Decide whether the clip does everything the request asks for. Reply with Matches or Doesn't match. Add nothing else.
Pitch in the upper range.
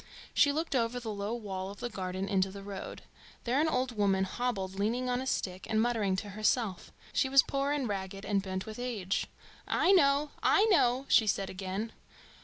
Matches